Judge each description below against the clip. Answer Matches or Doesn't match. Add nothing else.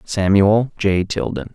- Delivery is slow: Matches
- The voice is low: Matches